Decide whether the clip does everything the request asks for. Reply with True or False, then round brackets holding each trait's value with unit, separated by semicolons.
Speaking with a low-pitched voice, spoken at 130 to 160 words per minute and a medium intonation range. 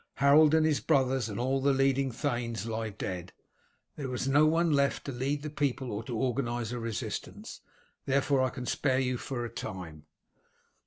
False (130 Hz; 175 wpm; 3.1 semitones)